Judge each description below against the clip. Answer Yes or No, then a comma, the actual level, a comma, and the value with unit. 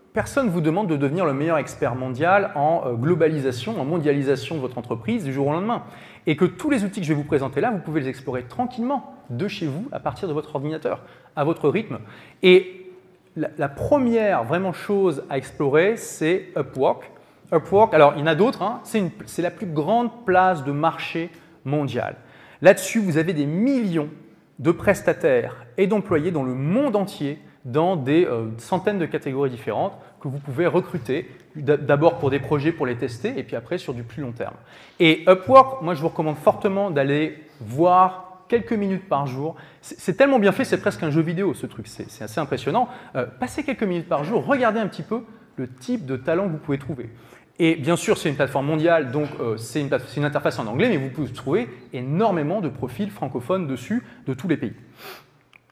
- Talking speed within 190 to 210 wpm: Yes, average, 195 wpm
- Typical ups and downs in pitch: No, wide, 5.7 semitones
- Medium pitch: Yes, medium, 165 Hz